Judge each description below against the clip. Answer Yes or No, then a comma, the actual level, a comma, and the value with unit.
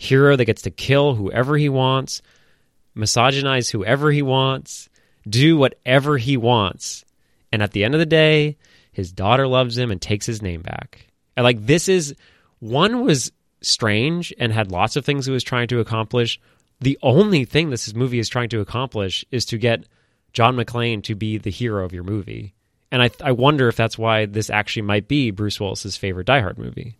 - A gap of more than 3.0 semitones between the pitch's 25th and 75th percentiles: Yes, average, 3.9 semitones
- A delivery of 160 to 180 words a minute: No, average, 190 wpm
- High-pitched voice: No, low, 120 Hz